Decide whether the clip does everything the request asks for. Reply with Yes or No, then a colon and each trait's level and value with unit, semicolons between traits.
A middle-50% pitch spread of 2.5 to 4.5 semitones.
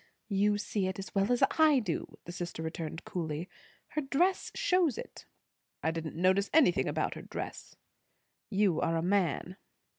No: average, 5.0 semitones